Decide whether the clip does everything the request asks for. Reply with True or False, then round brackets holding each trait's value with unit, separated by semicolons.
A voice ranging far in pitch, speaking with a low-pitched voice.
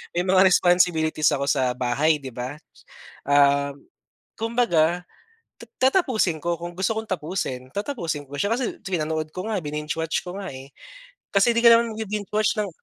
False (6.1 semitones; 175 Hz)